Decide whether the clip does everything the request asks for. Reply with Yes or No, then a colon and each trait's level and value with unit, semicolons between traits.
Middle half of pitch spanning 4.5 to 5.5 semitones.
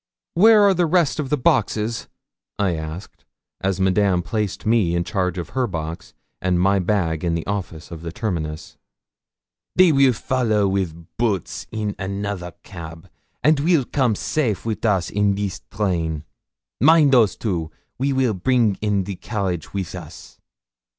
Yes: average, 5.2 semitones